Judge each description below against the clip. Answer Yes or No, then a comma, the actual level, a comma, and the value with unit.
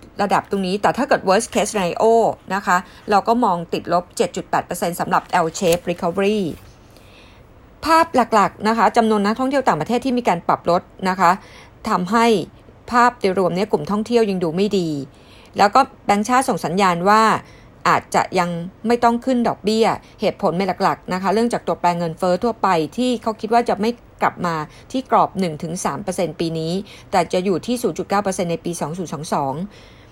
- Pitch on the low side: No, high, 195 Hz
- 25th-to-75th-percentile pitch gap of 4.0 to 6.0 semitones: Yes, average, 4.6 semitones